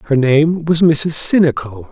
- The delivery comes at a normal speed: Yes, average, 155 wpm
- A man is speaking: Yes, male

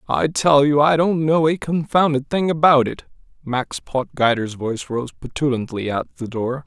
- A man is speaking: Yes, male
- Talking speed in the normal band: Yes, average, 170 wpm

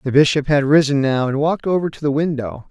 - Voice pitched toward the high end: No, medium, 145 Hz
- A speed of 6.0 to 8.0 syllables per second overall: Yes, 6.1 syllables/s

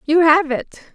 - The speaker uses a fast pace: No, average, 190 wpm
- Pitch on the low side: No, very high, 310 Hz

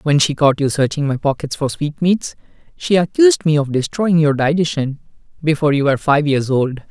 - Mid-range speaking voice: Yes, medium, 150 Hz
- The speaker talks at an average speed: Yes, average, 190 wpm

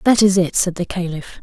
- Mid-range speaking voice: Yes, medium, 180 Hz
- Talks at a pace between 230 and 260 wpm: Yes, fast, 250 wpm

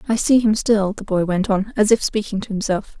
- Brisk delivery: Yes, fast, 260 wpm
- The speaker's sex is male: No, female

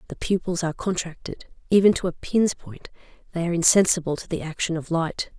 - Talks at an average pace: Yes, average, 190 wpm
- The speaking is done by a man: No, female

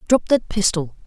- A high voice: Yes, high, 220 Hz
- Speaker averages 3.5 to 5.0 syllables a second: Yes, 4.9 syllables/s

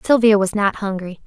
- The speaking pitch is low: No, high, 205 Hz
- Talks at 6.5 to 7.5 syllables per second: No, 5.3 syllables/s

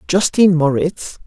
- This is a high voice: No, medium, 160 Hz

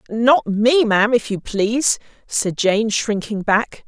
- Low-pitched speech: No, high, 220 Hz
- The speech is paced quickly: No, average, 155 wpm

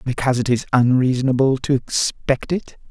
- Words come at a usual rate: Yes, average, 145 wpm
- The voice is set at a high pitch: No, low, 130 Hz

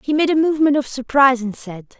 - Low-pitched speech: No, very high, 270 Hz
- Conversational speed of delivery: No, fast, 240 wpm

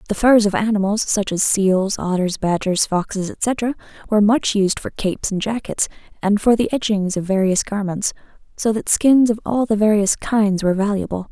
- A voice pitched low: No, high, 205 Hz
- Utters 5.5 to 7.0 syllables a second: No, 5.0 syllables/s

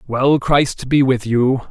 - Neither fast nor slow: Yes, average, 175 wpm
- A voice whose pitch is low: Yes, low, 130 Hz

